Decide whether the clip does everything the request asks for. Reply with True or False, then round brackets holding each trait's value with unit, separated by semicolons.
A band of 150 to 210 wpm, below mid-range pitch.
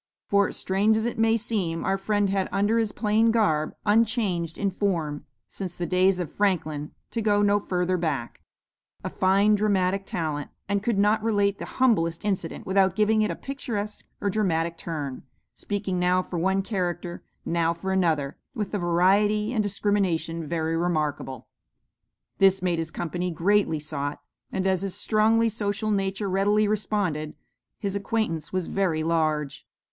False (160 wpm; 190 Hz)